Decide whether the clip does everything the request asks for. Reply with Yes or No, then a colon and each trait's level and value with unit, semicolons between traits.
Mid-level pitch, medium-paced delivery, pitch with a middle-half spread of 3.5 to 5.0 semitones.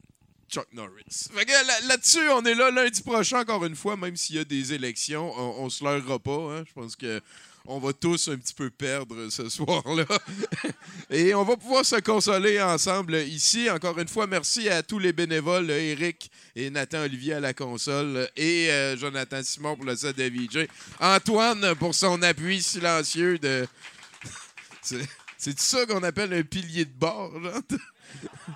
No: medium, 165 Hz; average, 175 wpm; wide, 5.6 semitones